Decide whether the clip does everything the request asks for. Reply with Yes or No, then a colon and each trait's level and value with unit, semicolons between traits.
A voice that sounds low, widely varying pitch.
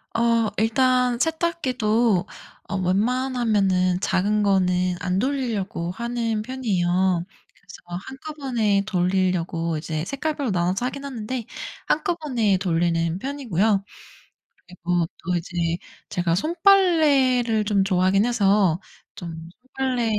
No: high, 210 Hz; wide, 5.8 semitones